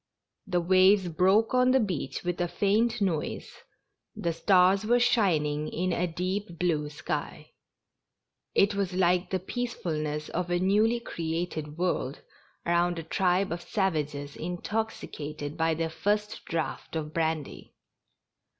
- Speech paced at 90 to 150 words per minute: Yes, average, 140 wpm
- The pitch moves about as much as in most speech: Yes, average, 3.6 semitones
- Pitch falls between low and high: Yes, medium, 175 Hz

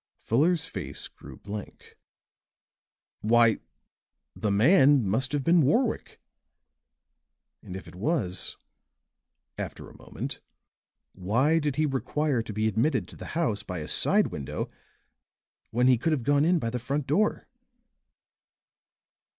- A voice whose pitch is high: No, low, 130 Hz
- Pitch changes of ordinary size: No, wide, 6.1 semitones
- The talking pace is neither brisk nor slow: No, slow, 130 wpm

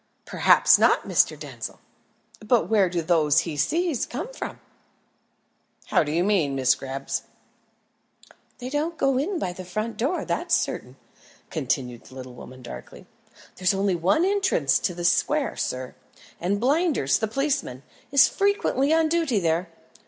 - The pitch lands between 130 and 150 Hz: No, high, 200 Hz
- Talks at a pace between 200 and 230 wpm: No, average, 150 wpm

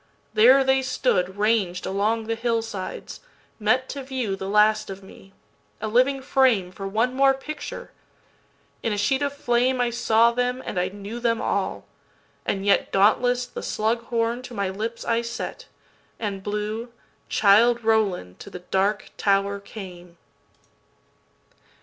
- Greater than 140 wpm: No, slow, 135 wpm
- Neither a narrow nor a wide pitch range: Yes, average, 3.7 semitones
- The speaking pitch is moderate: No, high, 225 Hz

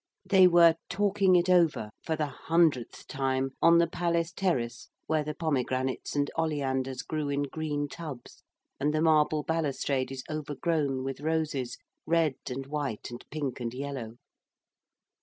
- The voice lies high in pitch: No, medium, 150 Hz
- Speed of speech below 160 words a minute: Yes, average, 145 wpm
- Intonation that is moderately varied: Yes, average, 3.6 semitones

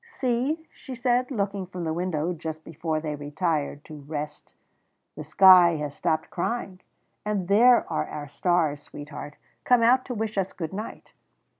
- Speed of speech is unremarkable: Yes, average, 160 wpm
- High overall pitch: No, medium, 175 Hz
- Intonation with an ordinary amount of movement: No, wide, 5.9 semitones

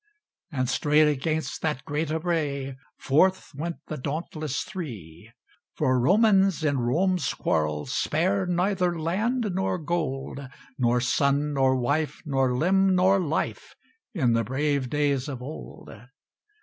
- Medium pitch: Yes, medium, 150 Hz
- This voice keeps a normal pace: No, slow, 125 wpm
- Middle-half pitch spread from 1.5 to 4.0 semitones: No, average, 4.9 semitones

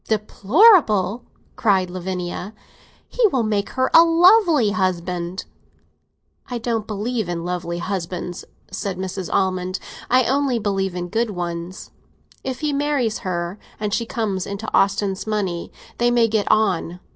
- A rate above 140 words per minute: No, slow, 135 wpm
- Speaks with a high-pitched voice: Yes, high, 200 Hz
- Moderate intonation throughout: Yes, average, 4.5 semitones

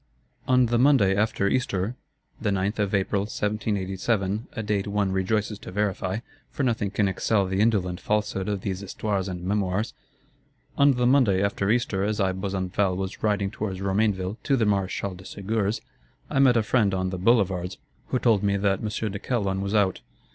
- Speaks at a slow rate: No, average, 175 wpm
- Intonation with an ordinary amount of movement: No, narrow, 2.2 semitones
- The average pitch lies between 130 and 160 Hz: No, low, 100 Hz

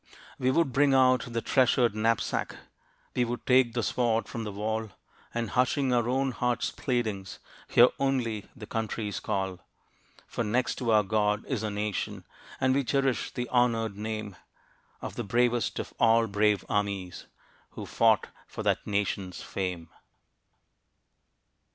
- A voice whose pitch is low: Yes, low, 115 Hz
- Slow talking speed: No, average, 145 wpm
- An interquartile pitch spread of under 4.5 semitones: Yes, average, 3.0 semitones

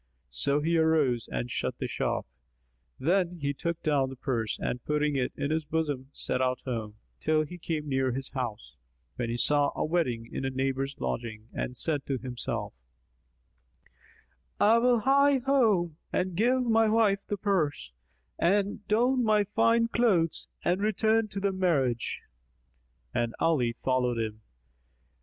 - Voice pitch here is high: No, medium, 155 Hz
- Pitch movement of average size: No, wide, 7.8 semitones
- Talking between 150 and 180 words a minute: Yes, average, 155 wpm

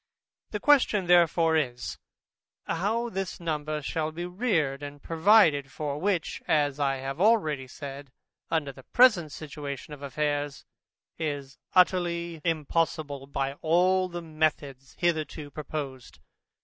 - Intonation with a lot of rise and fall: No, average, 3.5 semitones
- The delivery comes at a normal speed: No, slow, 125 wpm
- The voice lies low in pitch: No, medium, 155 Hz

